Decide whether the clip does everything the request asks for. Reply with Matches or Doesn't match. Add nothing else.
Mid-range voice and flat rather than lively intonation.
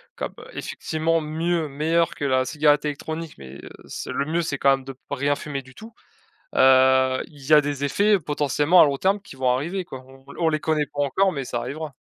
Doesn't match